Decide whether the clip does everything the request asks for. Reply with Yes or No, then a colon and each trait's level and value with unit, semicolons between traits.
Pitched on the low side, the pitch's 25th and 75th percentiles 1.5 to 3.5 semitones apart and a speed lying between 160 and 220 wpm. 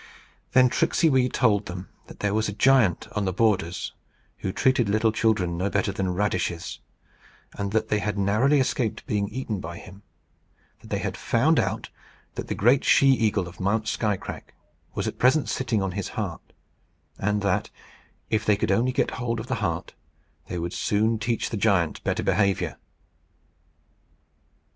Yes: low, 105 Hz; average, 3.1 semitones; average, 170 wpm